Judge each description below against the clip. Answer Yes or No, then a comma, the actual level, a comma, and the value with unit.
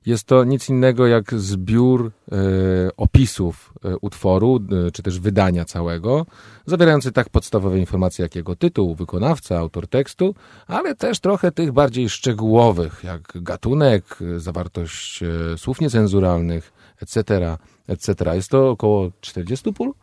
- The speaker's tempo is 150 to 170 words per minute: No, average, 130 wpm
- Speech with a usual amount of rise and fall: No, wide, 6.4 semitones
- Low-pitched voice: Yes, low, 100 Hz